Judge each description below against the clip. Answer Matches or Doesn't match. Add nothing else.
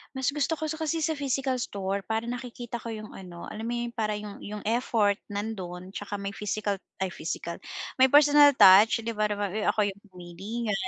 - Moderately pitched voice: Doesn't match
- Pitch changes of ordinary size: Matches